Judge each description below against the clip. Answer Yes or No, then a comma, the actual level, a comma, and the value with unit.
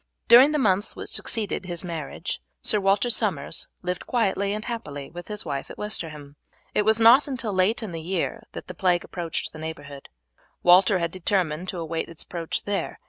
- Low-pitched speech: No, medium, 185 Hz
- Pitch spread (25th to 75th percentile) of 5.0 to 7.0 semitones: No, average, 4.4 semitones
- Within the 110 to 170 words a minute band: No, average, 190 wpm